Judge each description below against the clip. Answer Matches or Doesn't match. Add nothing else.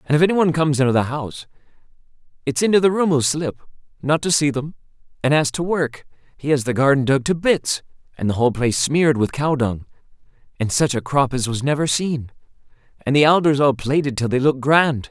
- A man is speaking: Matches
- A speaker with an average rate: Doesn't match